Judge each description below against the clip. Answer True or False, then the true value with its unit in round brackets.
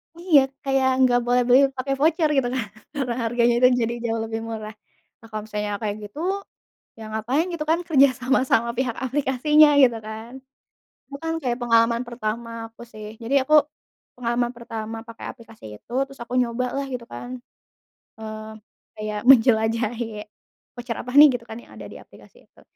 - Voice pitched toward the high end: True (240 Hz)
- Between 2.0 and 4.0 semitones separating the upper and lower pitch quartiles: True (2.9 semitones)